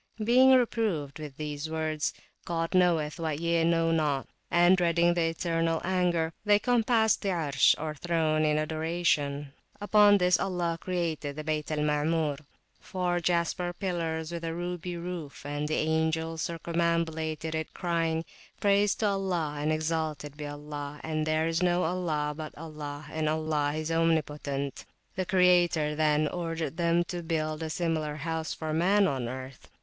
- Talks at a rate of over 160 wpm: No, average, 155 wpm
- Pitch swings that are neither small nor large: No, narrow, 2.3 semitones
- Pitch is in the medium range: Yes, medium, 160 Hz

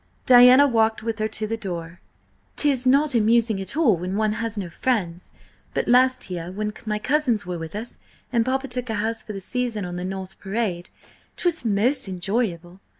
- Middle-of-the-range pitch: No, high, 220 Hz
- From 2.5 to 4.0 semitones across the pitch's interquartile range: No, average, 4.5 semitones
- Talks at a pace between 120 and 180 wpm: No, average, 190 wpm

